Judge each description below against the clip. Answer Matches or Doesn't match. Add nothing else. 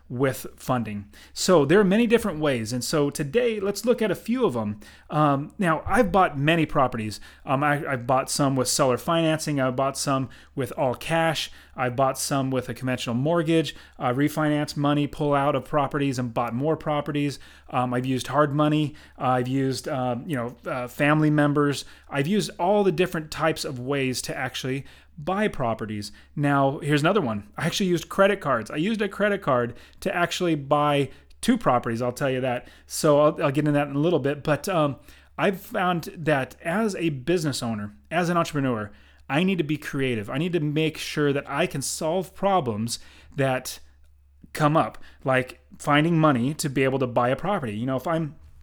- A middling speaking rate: Matches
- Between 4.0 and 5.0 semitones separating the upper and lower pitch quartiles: Matches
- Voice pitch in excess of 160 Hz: Doesn't match